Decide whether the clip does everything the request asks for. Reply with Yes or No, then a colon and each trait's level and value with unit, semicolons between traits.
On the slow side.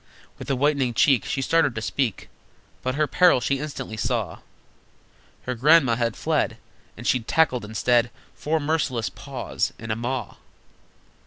No: average, 150 wpm